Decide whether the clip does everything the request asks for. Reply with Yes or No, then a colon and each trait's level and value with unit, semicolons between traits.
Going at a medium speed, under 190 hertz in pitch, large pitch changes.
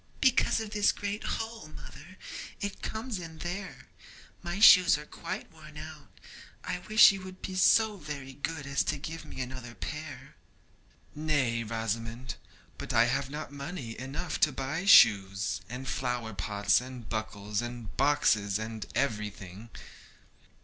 Yes: average, 145 wpm; medium, 140 Hz; wide, 7.2 semitones